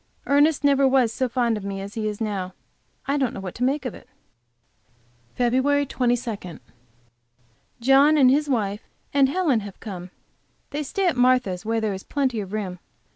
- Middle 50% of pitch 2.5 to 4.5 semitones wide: No, average, 5.0 semitones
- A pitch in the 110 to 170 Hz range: No, high, 245 Hz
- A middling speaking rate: Yes, average, 180 wpm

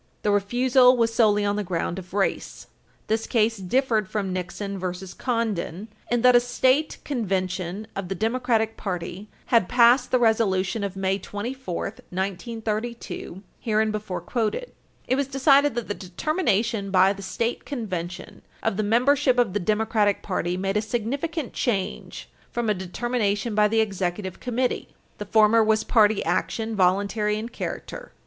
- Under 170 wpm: Yes, average, 155 wpm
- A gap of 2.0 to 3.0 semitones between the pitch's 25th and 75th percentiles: No, average, 3.6 semitones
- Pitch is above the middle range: Yes, high, 215 Hz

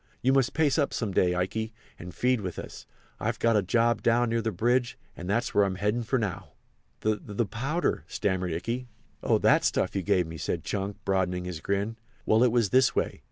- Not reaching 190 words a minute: No, fast, 205 wpm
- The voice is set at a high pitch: No, low, 110 Hz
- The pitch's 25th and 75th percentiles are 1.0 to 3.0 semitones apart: No, average, 4.2 semitones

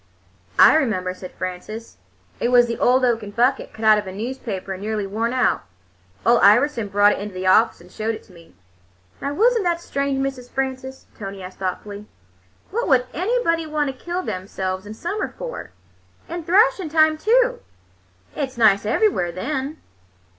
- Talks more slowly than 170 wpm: No, average, 175 wpm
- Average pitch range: No, wide, 7.2 semitones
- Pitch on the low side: No, high, 245 Hz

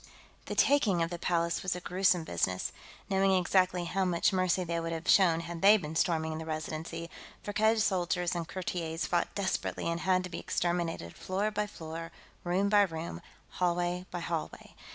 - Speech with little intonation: Yes, narrow, 2.1 semitones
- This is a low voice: No, medium, 175 Hz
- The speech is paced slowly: No, average, 175 wpm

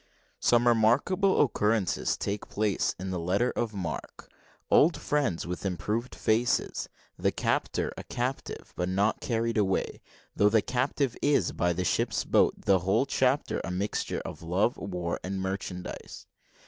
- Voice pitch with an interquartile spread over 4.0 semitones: Yes, average, 4.6 semitones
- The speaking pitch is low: Yes, low, 105 Hz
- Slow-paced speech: No, average, 150 wpm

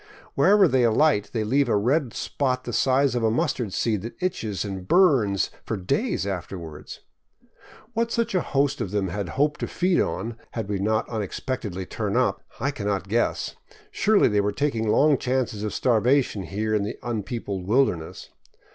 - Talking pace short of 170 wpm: No, average, 175 wpm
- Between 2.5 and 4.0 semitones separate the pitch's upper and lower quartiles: No, average, 5.2 semitones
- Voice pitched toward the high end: No, low, 115 Hz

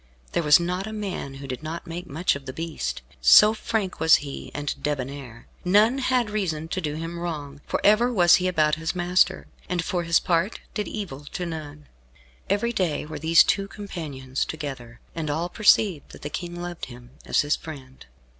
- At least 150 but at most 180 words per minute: No, average, 190 wpm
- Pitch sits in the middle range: Yes, medium, 165 Hz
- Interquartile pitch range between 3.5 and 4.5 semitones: Yes, average, 4.2 semitones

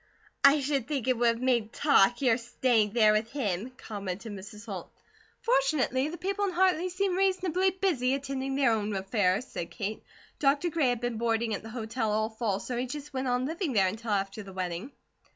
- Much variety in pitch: No, average, 4.9 semitones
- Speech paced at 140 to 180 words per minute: No, average, 200 wpm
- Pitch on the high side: Yes, high, 245 Hz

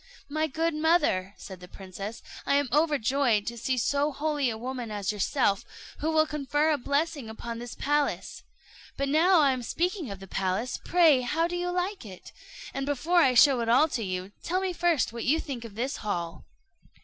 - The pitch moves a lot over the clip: Yes, wide, 5.7 semitones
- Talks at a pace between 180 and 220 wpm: Yes, average, 195 wpm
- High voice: Yes, very high, 275 Hz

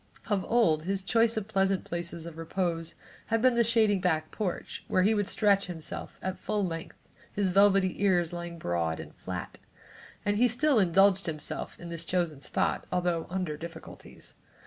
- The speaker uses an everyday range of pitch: Yes, average, 3.4 semitones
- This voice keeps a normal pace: Yes, average, 170 wpm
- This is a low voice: No, medium, 185 Hz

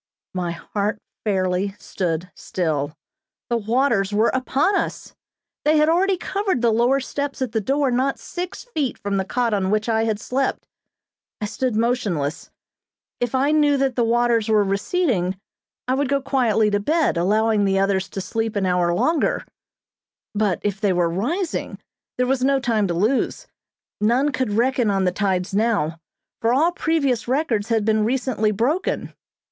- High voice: Yes, high, 225 Hz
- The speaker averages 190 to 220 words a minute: No, average, 165 wpm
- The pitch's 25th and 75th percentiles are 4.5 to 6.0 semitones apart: Yes, average, 5.1 semitones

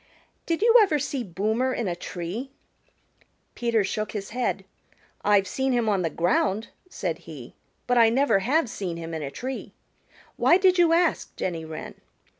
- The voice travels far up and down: Yes, wide, 6.7 semitones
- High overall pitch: Yes, high, 220 Hz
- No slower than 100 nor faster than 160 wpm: No, average, 170 wpm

